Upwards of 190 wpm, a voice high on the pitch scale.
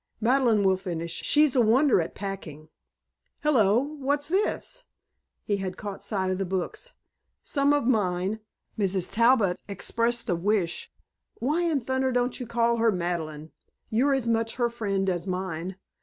No: average, 155 wpm; high, 220 Hz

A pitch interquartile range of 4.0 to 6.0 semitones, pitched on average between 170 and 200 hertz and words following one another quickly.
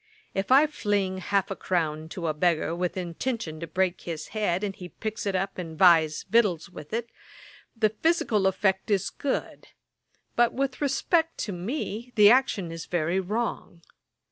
No: average, 4.6 semitones; high, 190 Hz; average, 170 wpm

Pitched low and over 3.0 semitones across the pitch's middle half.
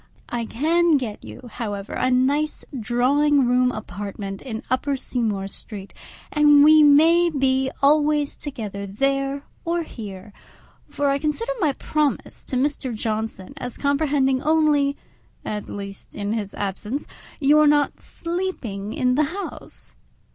No: very high, 270 Hz; average, 5.3 semitones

